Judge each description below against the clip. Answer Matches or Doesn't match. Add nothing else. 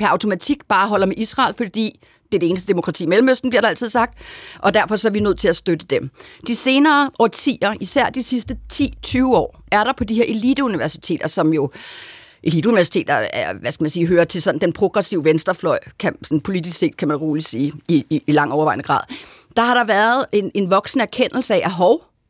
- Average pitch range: Doesn't match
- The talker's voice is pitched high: Matches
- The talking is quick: Doesn't match